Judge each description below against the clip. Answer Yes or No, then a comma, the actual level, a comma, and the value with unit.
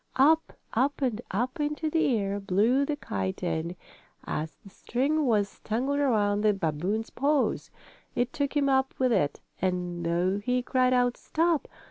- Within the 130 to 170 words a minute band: Yes, average, 160 wpm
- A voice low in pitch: No, high, 240 Hz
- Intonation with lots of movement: Yes, wide, 6.0 semitones